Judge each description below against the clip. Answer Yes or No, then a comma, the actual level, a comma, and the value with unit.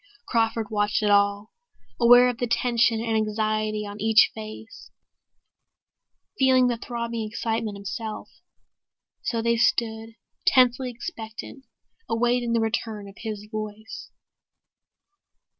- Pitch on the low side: No, high, 225 Hz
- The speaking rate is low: Yes, slow, 110 wpm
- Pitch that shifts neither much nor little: No, narrow, 1.7 semitones